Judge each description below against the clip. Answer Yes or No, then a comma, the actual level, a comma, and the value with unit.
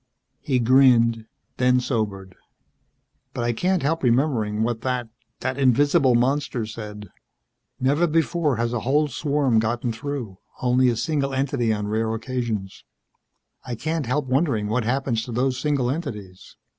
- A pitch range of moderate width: Yes, average, 3.7 semitones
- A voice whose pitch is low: Yes, low, 125 Hz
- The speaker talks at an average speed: Yes, average, 145 wpm